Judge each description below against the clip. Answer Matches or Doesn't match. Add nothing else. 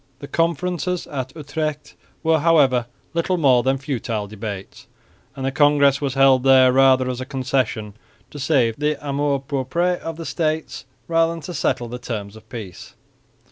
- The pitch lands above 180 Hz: Doesn't match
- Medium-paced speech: Matches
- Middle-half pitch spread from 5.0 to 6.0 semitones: Doesn't match